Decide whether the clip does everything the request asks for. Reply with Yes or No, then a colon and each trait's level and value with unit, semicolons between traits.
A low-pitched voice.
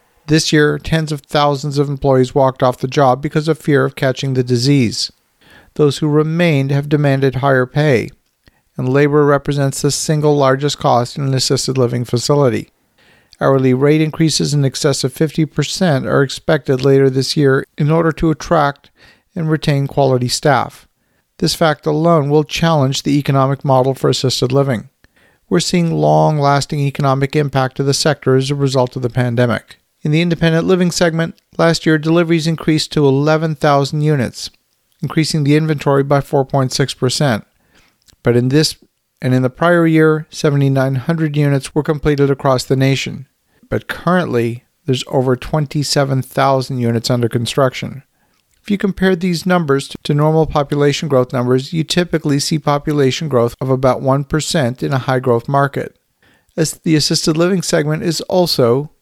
No: medium, 145 Hz